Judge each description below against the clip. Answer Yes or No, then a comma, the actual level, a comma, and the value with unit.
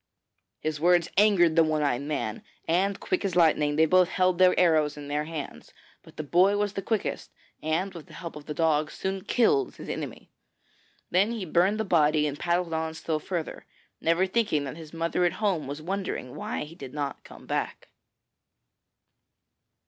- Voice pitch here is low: No, medium, 165 Hz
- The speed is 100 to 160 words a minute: No, average, 185 wpm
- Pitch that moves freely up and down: No, average, 3.6 semitones